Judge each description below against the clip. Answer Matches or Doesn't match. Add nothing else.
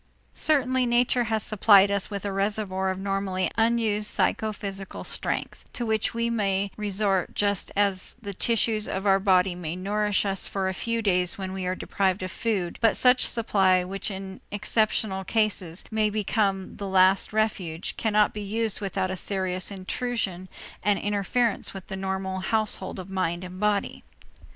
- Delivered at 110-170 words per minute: Matches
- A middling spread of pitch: Doesn't match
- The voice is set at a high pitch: Matches